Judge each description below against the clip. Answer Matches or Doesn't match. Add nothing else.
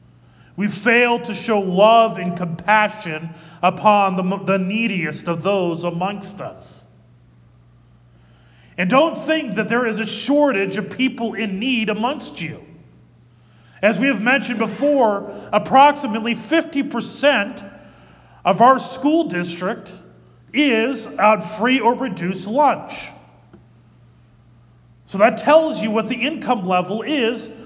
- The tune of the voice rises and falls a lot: Matches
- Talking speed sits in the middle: Doesn't match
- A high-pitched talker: Matches